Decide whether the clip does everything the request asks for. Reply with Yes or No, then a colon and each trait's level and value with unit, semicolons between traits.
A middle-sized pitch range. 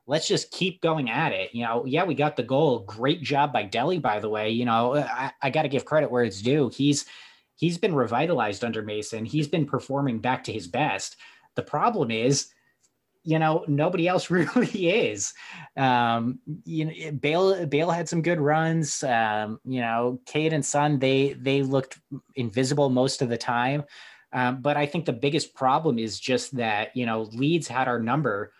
Yes: average, 4.0 semitones